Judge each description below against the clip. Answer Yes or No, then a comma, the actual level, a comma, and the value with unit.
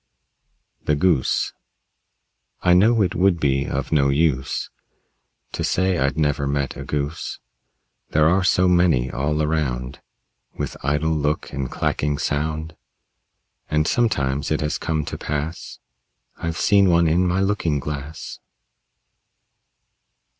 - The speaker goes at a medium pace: No, slow, 125 wpm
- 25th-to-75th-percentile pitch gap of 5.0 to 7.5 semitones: No, average, 3.5 semitones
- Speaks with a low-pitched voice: Yes, very low, 75 Hz